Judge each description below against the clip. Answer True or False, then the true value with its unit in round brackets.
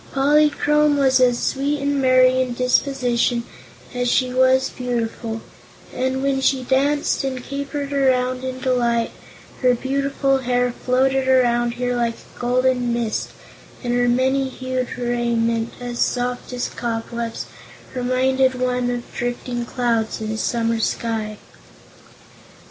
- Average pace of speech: False (130 wpm)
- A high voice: True (250 Hz)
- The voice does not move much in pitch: True (1.6 semitones)